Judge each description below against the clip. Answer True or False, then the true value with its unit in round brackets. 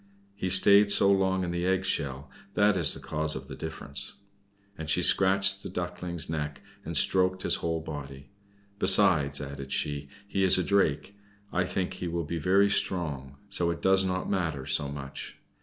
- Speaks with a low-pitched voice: True (85 Hz)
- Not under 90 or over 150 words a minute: False (180 wpm)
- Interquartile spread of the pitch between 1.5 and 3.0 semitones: False (4.5 semitones)